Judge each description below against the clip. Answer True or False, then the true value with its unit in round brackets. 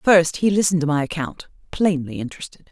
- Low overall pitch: False (165 Hz)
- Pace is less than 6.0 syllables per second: False (6.1 syllables/s)